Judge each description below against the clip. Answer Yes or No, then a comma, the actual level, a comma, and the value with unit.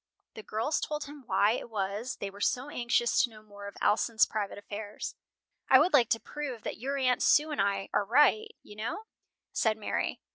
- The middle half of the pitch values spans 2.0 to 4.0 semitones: No, average, 5.0 semitones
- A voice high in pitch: Yes, high, 225 Hz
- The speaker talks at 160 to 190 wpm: No, fast, 205 wpm